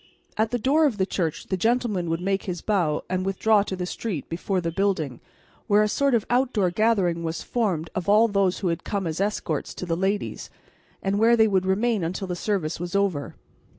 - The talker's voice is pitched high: Yes, high, 195 Hz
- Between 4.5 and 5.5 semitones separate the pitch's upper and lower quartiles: No, average, 3.6 semitones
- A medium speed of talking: No, fast, 215 wpm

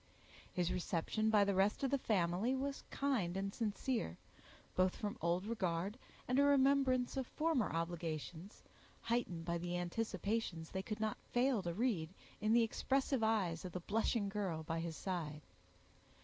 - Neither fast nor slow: Yes, average, 160 wpm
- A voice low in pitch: No, high, 200 Hz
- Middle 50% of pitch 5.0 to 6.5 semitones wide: Yes, wide, 5.5 semitones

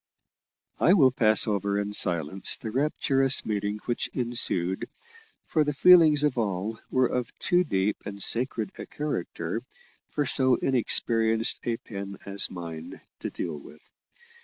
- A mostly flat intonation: No, average, 5.1 semitones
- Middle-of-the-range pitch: No, low, 115 Hz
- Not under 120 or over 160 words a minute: Yes, average, 140 wpm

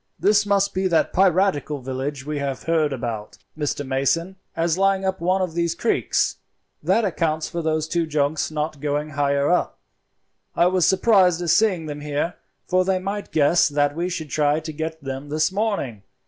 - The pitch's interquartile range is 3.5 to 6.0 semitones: Yes, average, 4.1 semitones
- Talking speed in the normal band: Yes, average, 180 wpm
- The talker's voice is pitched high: No, medium, 160 Hz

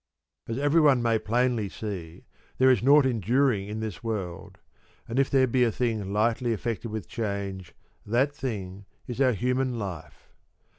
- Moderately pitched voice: No, low, 115 Hz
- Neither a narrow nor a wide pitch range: Yes, average, 3.9 semitones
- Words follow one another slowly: No, average, 160 wpm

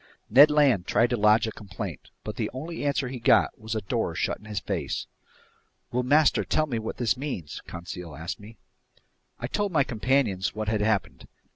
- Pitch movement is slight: No, average, 4.8 semitones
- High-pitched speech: No, low, 110 Hz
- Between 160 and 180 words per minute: No, average, 190 wpm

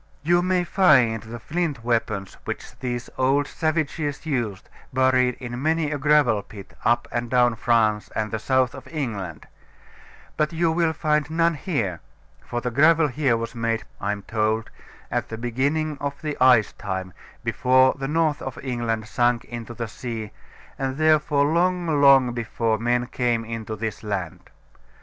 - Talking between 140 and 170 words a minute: Yes, average, 160 wpm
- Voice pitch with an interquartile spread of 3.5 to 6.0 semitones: Yes, average, 4.7 semitones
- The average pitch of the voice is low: Yes, low, 125 Hz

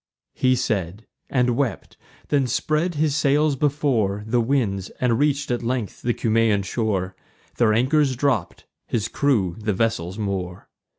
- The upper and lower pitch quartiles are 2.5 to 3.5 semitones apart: No, average, 5.2 semitones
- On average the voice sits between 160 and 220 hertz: No, low, 120 Hz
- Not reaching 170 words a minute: Yes, average, 140 wpm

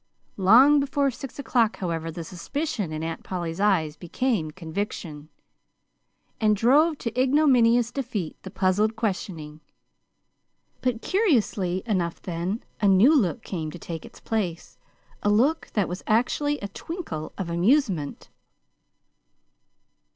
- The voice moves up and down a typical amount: No, wide, 6.7 semitones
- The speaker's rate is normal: No, slow, 125 wpm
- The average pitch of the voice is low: No, high, 205 Hz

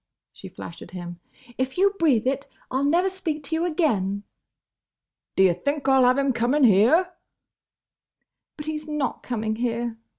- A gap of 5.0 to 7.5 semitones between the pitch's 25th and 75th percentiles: Yes, average, 5.3 semitones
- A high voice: Yes, very high, 265 Hz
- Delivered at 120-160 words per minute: No, average, 170 wpm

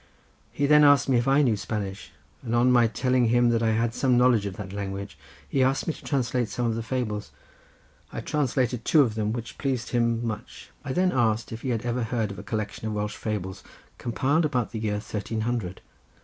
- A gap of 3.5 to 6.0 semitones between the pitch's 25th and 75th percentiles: No, average, 2.9 semitones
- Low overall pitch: Yes, low, 115 Hz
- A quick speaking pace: Yes, fast, 220 wpm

